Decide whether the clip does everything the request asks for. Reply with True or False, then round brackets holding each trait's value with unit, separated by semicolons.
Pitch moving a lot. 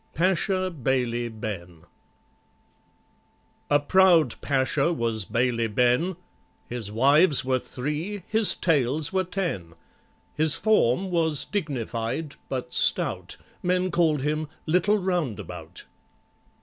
True (6.8 semitones)